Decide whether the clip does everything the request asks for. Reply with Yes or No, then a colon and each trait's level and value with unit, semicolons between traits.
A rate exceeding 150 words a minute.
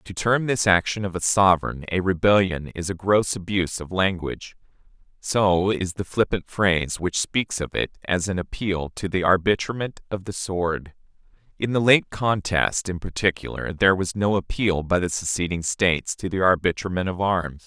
Yes: average, 175 wpm